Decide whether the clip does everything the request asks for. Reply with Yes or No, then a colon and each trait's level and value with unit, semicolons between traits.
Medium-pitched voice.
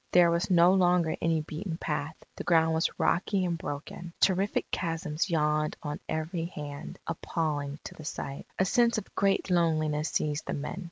Yes: medium, 165 Hz